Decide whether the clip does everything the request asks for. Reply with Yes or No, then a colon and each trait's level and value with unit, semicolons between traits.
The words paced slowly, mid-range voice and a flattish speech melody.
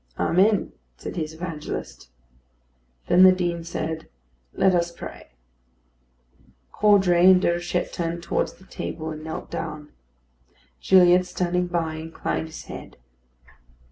Yes: slow, 115 wpm; medium, 175 Hz; narrow, 2.2 semitones